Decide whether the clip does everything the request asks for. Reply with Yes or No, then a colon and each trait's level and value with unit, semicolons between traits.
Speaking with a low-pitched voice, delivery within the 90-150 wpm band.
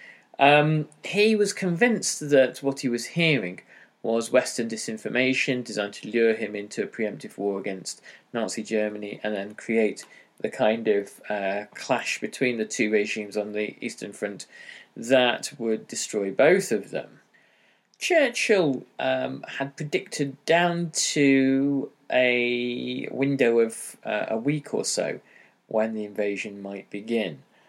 Yes: low, 115 Hz; average, 140 wpm